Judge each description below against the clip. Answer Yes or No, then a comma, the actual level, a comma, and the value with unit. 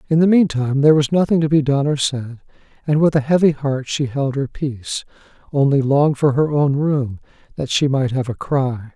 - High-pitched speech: No, medium, 140 Hz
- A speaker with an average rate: No, fast, 215 wpm